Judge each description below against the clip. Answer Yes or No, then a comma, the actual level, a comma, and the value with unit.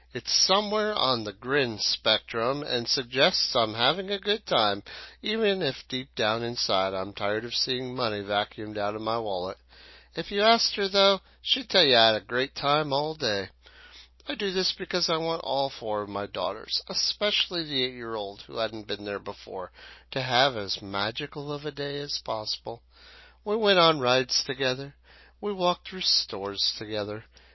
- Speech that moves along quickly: No, average, 175 wpm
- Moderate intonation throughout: No, wide, 8.9 semitones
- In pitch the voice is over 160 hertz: No, low, 130 Hz